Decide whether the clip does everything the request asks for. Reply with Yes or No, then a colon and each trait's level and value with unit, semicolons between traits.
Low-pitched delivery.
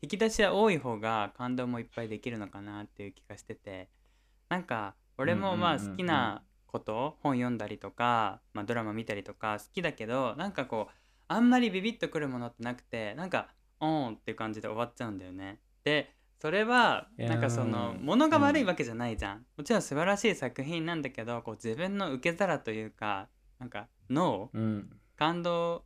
Yes: low, 120 Hz